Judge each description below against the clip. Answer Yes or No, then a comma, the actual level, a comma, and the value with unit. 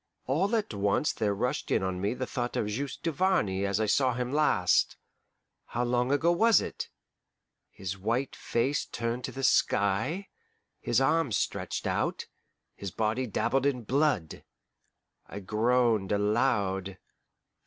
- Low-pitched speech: Yes, low, 120 Hz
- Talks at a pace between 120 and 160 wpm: Yes, average, 145 wpm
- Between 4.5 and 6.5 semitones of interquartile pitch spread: Yes, average, 5.2 semitones